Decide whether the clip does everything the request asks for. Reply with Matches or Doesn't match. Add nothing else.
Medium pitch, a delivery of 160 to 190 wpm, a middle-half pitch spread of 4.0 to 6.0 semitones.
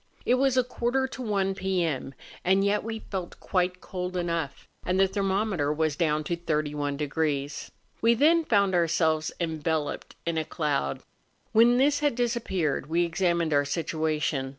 Doesn't match